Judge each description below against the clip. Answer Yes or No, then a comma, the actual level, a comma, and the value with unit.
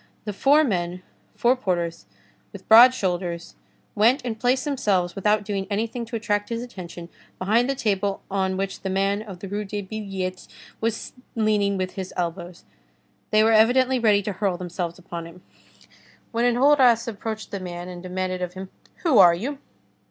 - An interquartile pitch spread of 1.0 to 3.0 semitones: No, average, 3.8 semitones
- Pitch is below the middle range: No, high, 200 Hz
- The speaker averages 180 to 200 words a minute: No, average, 170 wpm